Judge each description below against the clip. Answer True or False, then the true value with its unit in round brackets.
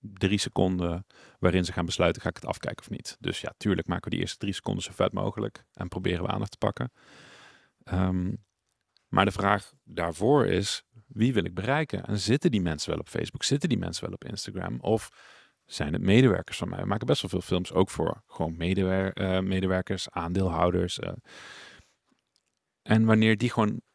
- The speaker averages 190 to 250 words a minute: True (195 wpm)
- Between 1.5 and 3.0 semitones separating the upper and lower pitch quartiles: True (2.6 semitones)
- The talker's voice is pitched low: True (95 Hz)